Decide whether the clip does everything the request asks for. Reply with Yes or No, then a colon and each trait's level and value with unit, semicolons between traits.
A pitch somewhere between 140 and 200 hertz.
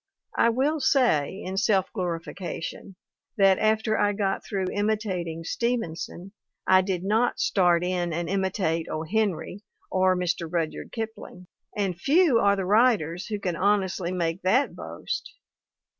Yes: high, 190 Hz